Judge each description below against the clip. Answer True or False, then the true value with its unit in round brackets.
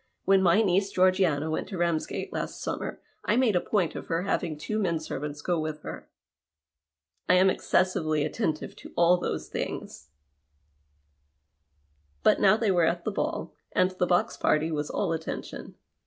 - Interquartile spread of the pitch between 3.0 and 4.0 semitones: True (3.4 semitones)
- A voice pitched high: False (175 Hz)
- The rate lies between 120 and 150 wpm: False (165 wpm)